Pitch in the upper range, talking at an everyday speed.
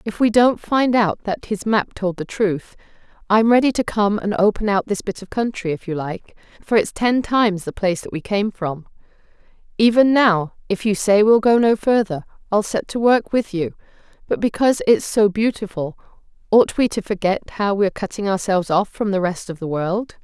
No: high, 205 Hz; fast, 210 wpm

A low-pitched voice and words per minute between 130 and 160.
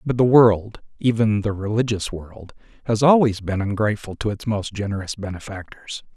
Yes: low, 105 Hz; average, 155 wpm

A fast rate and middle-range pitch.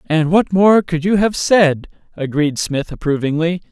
No: average, 160 wpm; medium, 170 Hz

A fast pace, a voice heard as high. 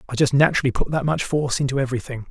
No: fast, 235 wpm; low, 135 Hz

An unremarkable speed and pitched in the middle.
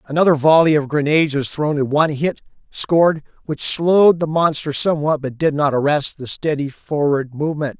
Yes: average, 175 wpm; medium, 150 Hz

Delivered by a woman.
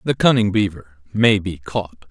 No: male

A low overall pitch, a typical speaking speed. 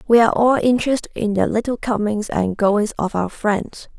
No: high, 220 Hz; average, 195 wpm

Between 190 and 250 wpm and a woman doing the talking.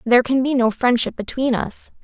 Yes: fast, 205 wpm; female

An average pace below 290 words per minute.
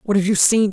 No: fast, 335 wpm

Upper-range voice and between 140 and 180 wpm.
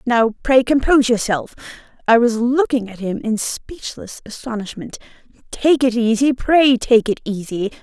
Yes: high, 240 Hz; average, 145 wpm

